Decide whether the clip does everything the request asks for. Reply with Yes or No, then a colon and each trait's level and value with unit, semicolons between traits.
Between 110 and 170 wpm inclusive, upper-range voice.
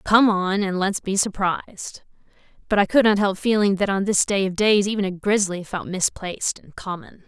No: fast, 205 wpm; high, 195 Hz